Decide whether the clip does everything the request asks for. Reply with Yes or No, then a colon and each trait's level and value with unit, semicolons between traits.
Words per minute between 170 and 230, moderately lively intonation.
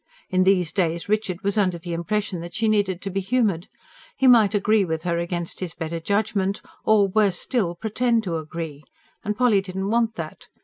Yes: average, 190 wpm; average, 3.8 semitones